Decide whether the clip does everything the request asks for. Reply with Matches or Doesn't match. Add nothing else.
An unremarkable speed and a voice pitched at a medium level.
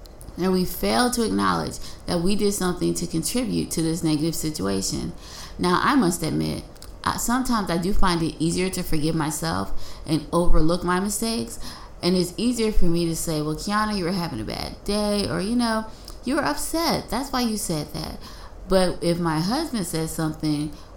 Matches